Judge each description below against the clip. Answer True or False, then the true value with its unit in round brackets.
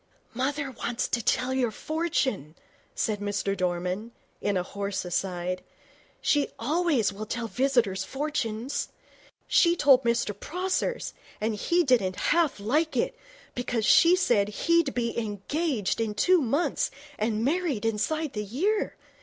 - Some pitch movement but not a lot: False (6.6 semitones)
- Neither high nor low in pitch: False (235 Hz)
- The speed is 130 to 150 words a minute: True (135 wpm)